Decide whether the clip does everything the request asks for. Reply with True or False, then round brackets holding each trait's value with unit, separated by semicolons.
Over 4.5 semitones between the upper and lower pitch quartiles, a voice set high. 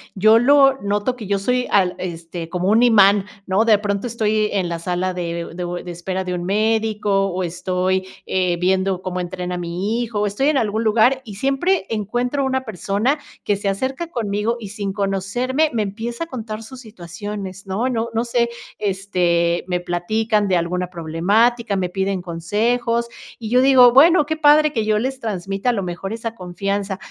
False (4.1 semitones; 205 Hz)